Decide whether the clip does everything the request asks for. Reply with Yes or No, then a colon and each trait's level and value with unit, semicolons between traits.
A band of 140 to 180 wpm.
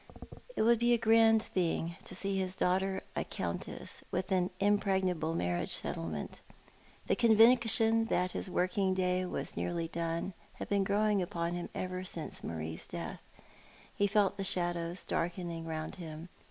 Yes: average, 155 wpm